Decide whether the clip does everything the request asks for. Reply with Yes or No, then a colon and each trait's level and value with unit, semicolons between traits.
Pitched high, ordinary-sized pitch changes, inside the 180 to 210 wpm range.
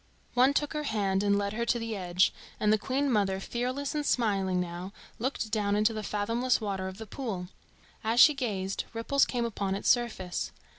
Yes: high, 215 Hz; average, 3.9 semitones; average, 200 wpm